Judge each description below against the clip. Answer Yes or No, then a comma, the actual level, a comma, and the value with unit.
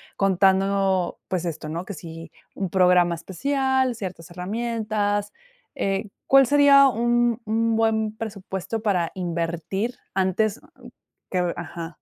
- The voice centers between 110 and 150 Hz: No, high, 195 Hz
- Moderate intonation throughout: Yes, average, 4.0 semitones